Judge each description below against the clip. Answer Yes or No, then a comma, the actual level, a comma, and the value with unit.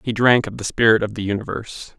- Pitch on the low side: Yes, low, 110 Hz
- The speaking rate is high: Yes, fast, 240 wpm